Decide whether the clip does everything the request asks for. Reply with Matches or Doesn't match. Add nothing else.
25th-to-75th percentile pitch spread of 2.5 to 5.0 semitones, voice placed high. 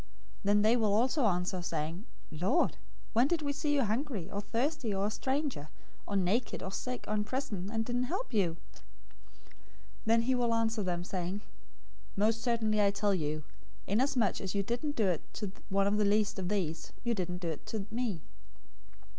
Matches